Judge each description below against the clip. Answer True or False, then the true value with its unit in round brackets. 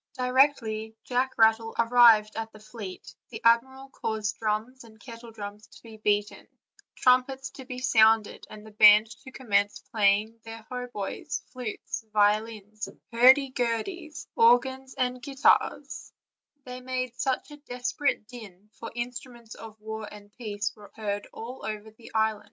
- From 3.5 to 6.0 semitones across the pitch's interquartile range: False (2.8 semitones)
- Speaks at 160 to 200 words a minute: False (140 wpm)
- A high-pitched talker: True (225 Hz)